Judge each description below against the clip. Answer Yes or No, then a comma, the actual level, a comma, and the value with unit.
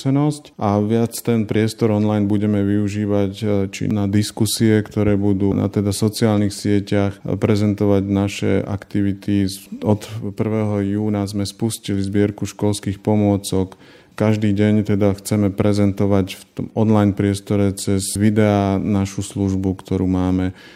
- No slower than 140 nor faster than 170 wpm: No, average, 120 wpm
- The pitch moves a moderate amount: No, narrow, 1.2 semitones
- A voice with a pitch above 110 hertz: No, low, 100 Hz